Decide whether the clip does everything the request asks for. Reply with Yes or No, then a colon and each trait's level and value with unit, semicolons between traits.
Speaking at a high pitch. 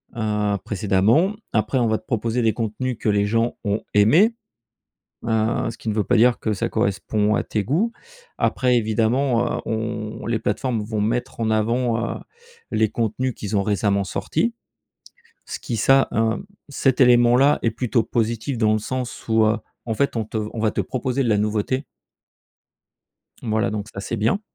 No: low, 115 Hz